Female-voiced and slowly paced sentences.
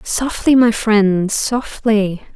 Yes: female; slow, 75 wpm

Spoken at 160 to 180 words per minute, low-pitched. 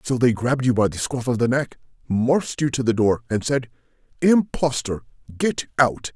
No: average, 195 wpm; low, 125 Hz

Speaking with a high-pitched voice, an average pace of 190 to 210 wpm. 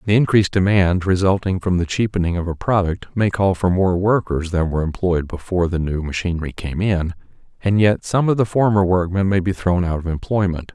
No: very low, 95 Hz; fast, 205 wpm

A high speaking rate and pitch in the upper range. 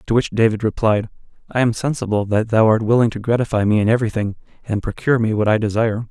No: fast, 225 wpm; low, 110 Hz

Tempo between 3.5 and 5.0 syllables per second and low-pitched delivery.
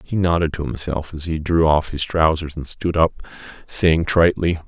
Yes: 4.9 syllables/s; very low, 80 Hz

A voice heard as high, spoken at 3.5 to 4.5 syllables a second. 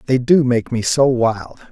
No: low, 120 Hz; 4.2 syllables/s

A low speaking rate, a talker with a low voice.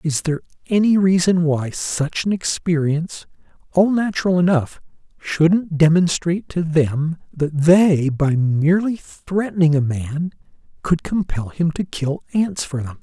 No: slow, 130 wpm; medium, 165 Hz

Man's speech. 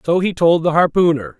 Yes: male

